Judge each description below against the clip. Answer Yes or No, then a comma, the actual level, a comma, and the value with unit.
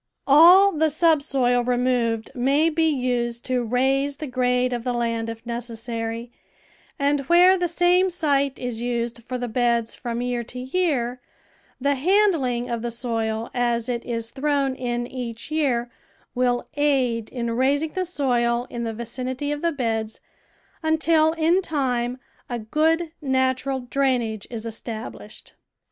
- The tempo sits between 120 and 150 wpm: Yes, average, 145 wpm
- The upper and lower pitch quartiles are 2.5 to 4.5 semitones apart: Yes, average, 3.5 semitones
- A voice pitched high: Yes, very high, 250 Hz